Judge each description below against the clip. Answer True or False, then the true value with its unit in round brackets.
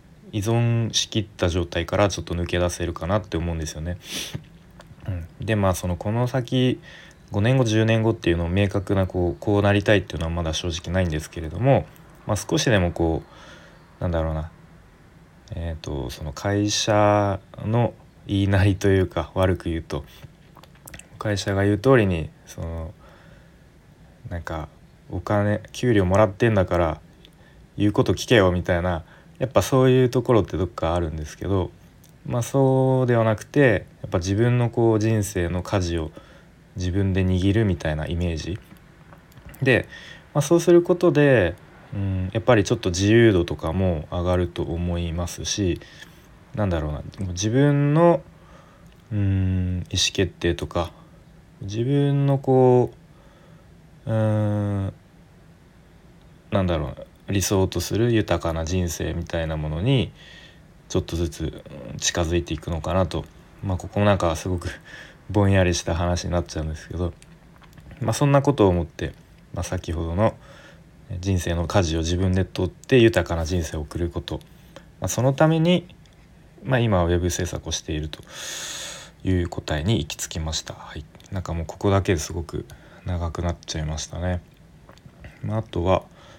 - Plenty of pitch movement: False (4.4 semitones)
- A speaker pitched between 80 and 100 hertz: True (95 Hz)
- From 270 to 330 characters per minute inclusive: True (305 characters per minute)